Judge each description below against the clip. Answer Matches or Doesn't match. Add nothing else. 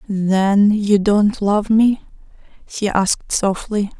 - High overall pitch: Matches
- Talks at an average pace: Doesn't match